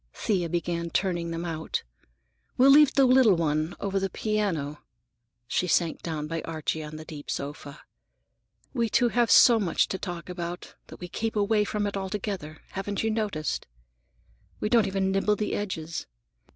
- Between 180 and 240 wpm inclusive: No, average, 165 wpm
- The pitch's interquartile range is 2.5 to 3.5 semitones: No, average, 4.5 semitones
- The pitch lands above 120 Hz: Yes, medium, 185 Hz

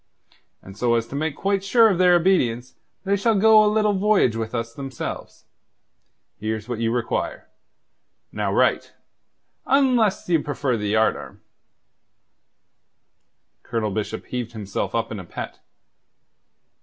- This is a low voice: Yes, low, 130 Hz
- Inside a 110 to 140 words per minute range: Yes, slow, 135 wpm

